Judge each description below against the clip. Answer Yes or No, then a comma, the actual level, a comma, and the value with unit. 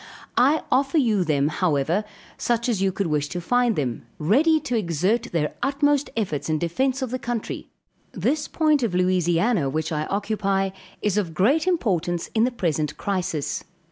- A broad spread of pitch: Yes, wide, 6.9 semitones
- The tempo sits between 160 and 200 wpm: Yes, average, 170 wpm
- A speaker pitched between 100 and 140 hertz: No, high, 195 Hz